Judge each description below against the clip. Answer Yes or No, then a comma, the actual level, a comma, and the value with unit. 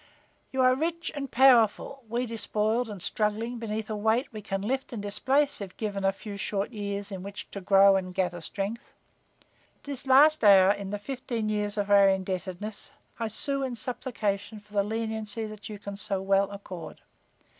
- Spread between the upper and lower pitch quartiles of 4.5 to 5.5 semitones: No, average, 2.9 semitones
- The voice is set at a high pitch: Yes, high, 210 Hz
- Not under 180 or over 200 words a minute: Yes, average, 185 wpm